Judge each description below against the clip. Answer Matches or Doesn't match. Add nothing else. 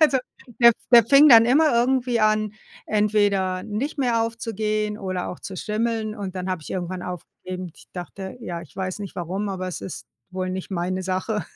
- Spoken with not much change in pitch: Doesn't match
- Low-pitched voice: Doesn't match